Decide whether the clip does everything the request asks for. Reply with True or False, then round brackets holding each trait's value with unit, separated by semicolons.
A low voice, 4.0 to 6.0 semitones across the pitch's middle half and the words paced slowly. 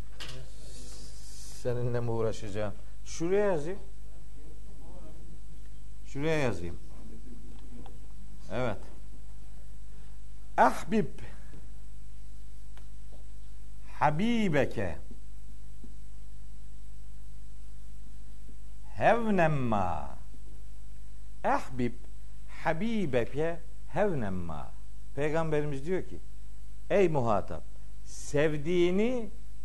True (120 Hz; 5.0 semitones; 40 wpm)